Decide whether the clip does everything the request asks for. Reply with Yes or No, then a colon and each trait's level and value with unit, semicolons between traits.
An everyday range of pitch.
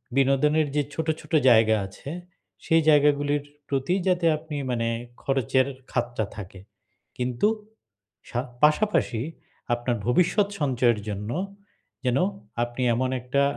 Yes: average, 3.7 semitones